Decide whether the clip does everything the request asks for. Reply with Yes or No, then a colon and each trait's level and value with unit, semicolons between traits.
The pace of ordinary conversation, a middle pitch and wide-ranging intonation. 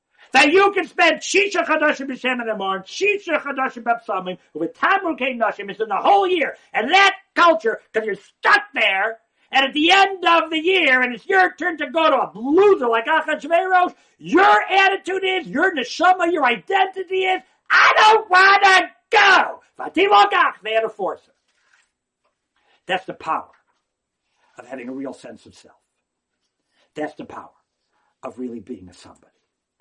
No: average, 165 wpm; very high, 335 Hz; wide, 7.5 semitones